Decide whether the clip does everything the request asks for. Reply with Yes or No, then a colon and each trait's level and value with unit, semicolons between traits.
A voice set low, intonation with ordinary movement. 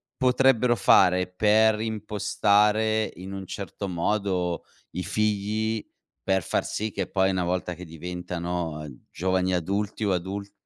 Yes: very low, 95 Hz; average, 3.0 semitones